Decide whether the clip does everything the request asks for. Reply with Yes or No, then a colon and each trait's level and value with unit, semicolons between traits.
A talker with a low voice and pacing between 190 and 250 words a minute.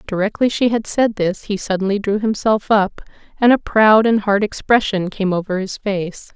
No: high, 205 Hz; average, 200 wpm